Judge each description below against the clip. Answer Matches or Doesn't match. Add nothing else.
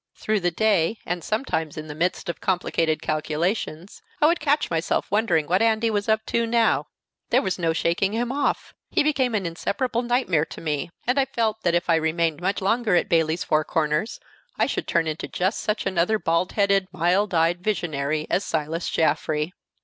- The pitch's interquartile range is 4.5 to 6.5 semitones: Matches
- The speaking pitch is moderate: Matches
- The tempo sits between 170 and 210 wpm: Matches